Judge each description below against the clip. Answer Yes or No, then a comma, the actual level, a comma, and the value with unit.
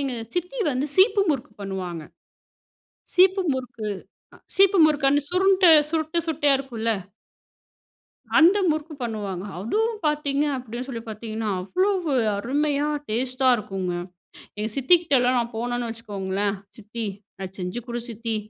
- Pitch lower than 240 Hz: No, very high, 255 Hz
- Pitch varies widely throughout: Yes, wide, 6.2 semitones